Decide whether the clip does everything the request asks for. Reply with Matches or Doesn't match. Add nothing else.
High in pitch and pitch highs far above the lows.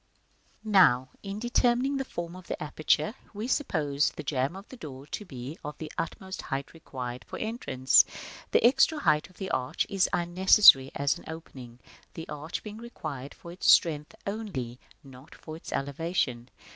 Doesn't match